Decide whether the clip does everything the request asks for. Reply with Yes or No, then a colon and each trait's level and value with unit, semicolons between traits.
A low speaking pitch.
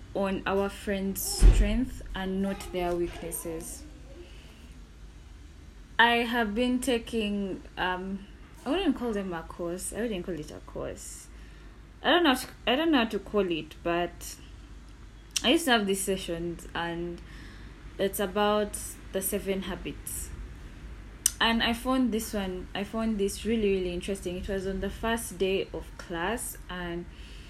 No: high, 190 Hz